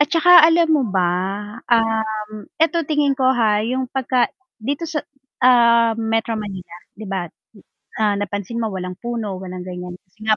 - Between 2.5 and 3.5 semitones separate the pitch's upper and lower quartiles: No, average, 4.4 semitones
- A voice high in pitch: Yes, high, 225 Hz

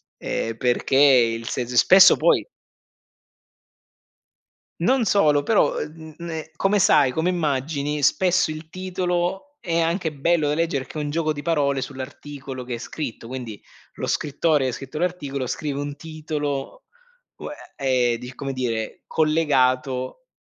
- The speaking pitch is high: No, medium, 145 Hz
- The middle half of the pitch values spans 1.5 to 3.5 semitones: No, average, 4.1 semitones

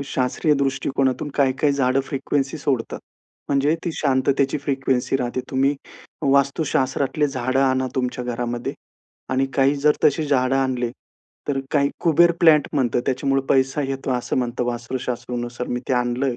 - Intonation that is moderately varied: No, narrow, 1.9 semitones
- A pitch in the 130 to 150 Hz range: Yes, low, 135 Hz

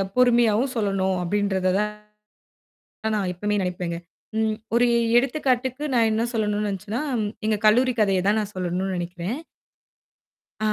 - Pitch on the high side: Yes, high, 210 Hz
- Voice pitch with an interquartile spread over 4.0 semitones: No, average, 3.7 semitones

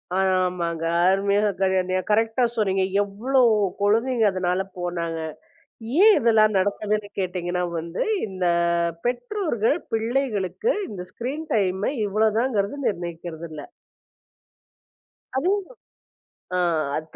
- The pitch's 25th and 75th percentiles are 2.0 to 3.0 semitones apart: No, average, 4.3 semitones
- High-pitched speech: Yes, high, 200 Hz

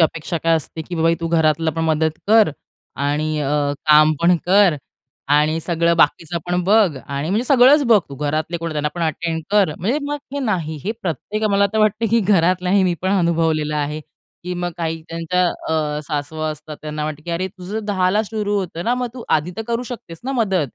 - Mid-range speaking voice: Yes, medium, 170 Hz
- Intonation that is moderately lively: Yes, average, 4.4 semitones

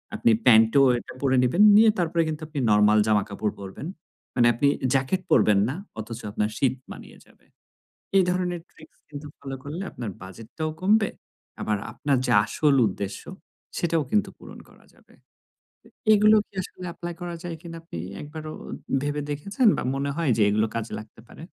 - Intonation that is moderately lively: No, wide, 7.5 semitones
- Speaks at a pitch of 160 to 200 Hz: No, medium, 145 Hz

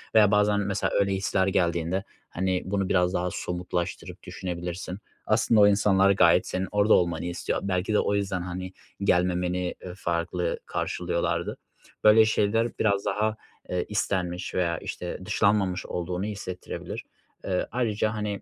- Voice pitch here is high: No, very low, 95 Hz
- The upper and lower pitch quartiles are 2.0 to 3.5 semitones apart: Yes, narrow, 2.4 semitones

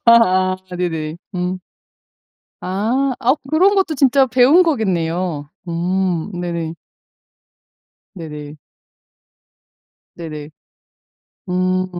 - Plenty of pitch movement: Yes, wide, 6.7 semitones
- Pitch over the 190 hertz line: No, medium, 185 Hz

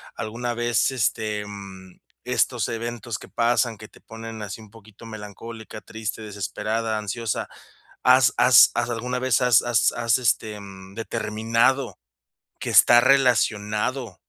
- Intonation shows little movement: Yes, narrow, 2.1 semitones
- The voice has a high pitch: No, low, 115 Hz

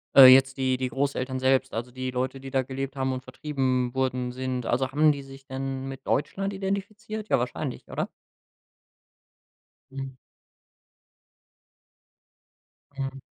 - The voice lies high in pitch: No, low, 135 Hz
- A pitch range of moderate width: No, narrow, 1.1 semitones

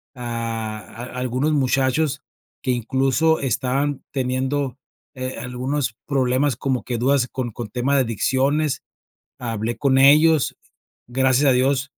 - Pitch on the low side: Yes, low, 130 Hz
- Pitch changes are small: Yes, narrow, 2.1 semitones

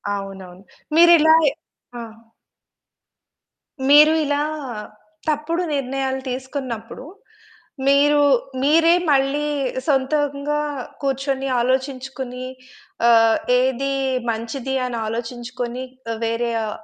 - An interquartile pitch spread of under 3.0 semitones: No, average, 3.4 semitones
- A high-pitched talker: Yes, very high, 265 Hz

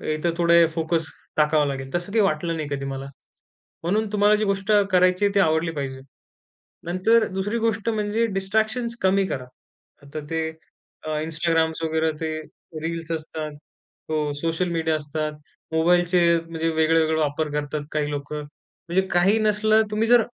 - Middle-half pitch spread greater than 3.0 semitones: Yes, average, 4.1 semitones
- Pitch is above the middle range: No, medium, 165 Hz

